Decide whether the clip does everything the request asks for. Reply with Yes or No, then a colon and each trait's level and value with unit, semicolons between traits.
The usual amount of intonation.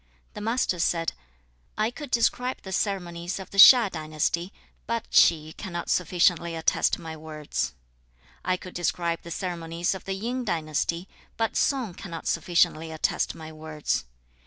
Yes: average, 3.4 semitones